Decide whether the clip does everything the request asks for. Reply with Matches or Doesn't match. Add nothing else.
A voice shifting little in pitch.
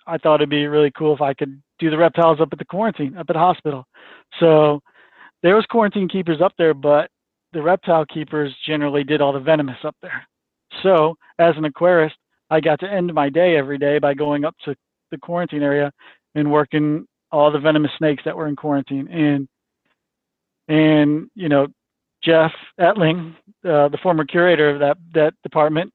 Matches